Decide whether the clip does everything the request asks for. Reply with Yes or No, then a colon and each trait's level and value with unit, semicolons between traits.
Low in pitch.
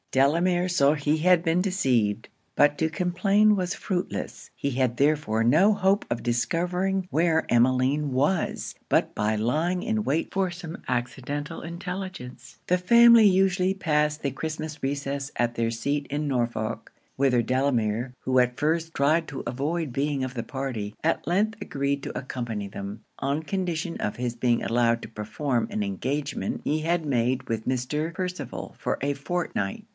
No: medium, 145 Hz